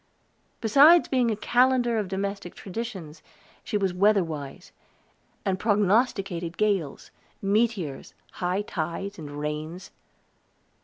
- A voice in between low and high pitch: No, high, 195 Hz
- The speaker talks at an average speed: No, slow, 105 wpm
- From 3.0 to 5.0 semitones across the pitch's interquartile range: Yes, average, 4.3 semitones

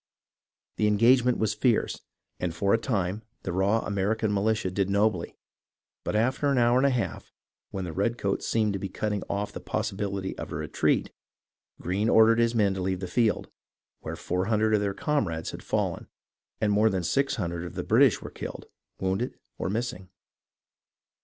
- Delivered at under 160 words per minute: No, average, 170 wpm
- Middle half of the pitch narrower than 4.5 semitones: Yes, average, 3.1 semitones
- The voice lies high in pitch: No, low, 105 Hz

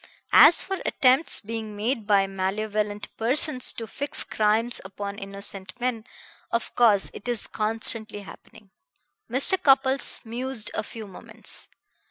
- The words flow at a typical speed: No, slow, 130 wpm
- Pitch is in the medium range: No, high, 220 Hz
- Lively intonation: No, average, 3.5 semitones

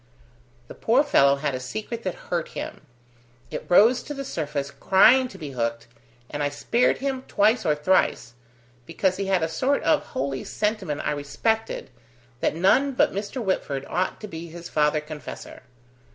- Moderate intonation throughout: No, wide, 7.1 semitones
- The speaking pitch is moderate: Yes, medium, 175 Hz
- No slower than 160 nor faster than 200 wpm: Yes, average, 170 wpm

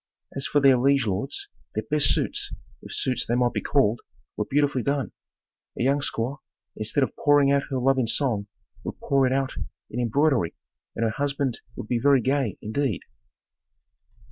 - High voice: No, low, 135 Hz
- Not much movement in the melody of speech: No, average, 3.1 semitones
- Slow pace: No, average, 175 wpm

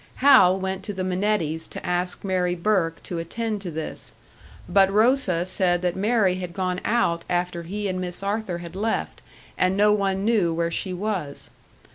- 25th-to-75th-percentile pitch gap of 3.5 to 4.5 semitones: No, average, 2.7 semitones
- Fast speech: No, average, 175 wpm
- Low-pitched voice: No, medium, 185 Hz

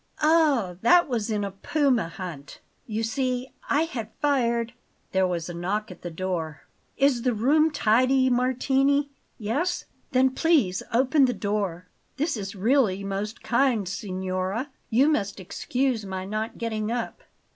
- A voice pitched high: Yes, high, 230 Hz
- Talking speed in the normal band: Yes, average, 150 wpm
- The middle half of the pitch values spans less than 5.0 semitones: No, wide, 5.4 semitones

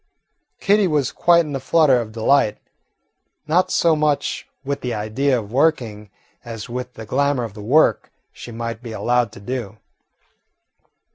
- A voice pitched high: No, low, 125 Hz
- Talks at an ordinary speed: Yes, average, 155 wpm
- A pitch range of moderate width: Yes, average, 4.3 semitones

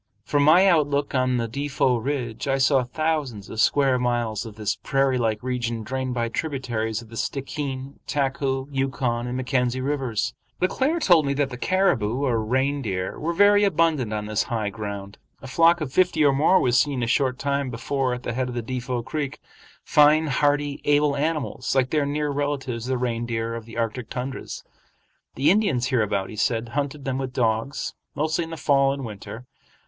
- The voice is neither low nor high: No, low, 130 Hz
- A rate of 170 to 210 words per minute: Yes, average, 185 wpm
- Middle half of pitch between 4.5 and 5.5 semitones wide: No, average, 3.5 semitones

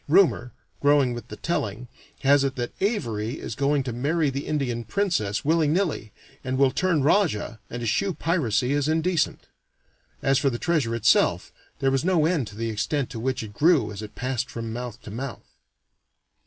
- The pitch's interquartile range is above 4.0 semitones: Yes, average, 5.0 semitones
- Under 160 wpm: No, average, 180 wpm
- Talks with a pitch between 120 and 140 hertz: Yes, low, 135 Hz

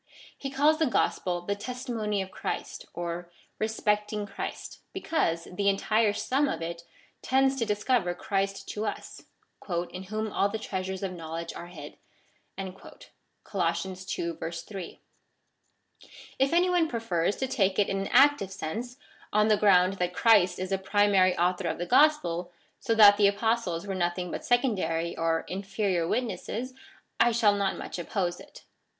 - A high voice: Yes, high, 200 Hz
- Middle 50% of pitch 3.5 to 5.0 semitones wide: Yes, average, 4.0 semitones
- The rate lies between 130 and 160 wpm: Yes, average, 155 wpm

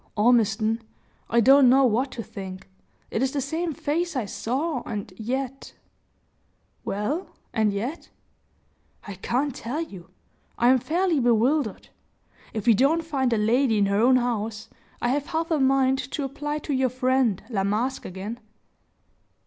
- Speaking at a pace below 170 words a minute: Yes, average, 160 wpm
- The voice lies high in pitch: Yes, very high, 250 Hz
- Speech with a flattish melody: No, average, 4.3 semitones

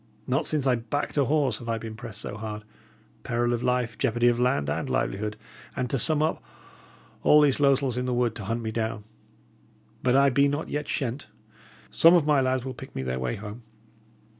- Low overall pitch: Yes, low, 125 Hz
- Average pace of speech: No, fast, 210 wpm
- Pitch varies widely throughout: No, average, 3.7 semitones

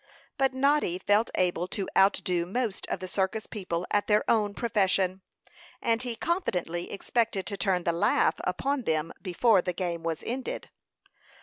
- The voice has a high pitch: Yes, high, 195 Hz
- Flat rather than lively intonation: No, average, 4.3 semitones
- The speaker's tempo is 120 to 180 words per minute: Yes, average, 160 wpm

